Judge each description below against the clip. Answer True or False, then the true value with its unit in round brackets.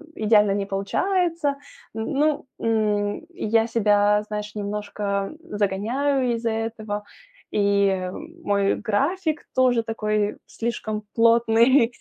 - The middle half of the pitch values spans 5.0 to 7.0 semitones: False (2.7 semitones)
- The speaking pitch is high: True (220 Hz)